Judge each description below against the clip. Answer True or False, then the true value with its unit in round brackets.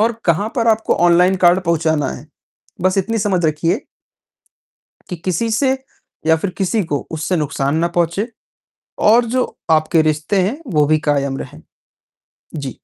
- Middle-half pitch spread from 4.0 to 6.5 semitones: True (5.2 semitones)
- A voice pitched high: False (175 Hz)